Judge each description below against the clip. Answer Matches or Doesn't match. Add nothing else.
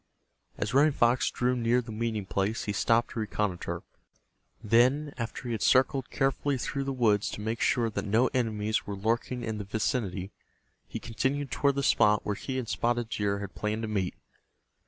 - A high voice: Doesn't match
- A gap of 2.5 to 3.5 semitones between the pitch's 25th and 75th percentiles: Matches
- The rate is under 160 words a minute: Doesn't match